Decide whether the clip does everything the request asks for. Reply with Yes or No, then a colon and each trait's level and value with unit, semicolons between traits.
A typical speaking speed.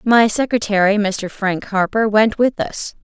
Yes: average, 155 wpm